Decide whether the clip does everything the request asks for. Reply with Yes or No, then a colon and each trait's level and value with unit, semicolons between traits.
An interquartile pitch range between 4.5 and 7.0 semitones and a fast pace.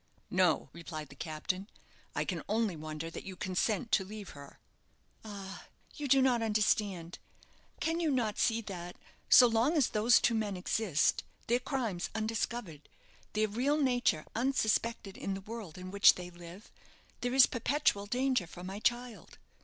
No: average, 4.8 semitones; average, 160 wpm